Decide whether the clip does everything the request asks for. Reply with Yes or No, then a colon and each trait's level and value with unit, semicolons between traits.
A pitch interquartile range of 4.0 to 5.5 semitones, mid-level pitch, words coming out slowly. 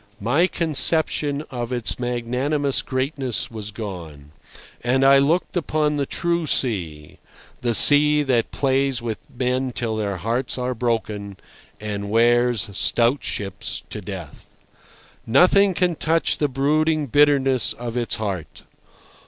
No: average, 4.4 semitones; low, 125 Hz; slow, 125 wpm